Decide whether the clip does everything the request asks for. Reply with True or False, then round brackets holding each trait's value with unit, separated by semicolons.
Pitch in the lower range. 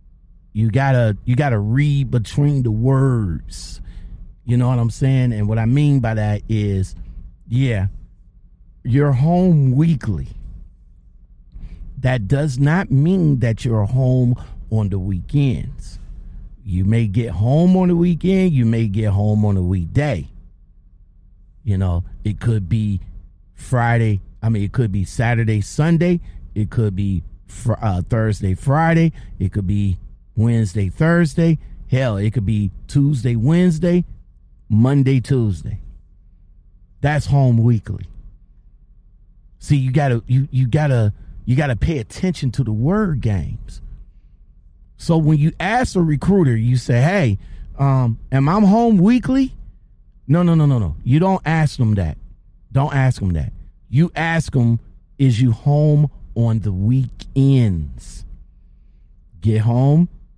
True (115 Hz)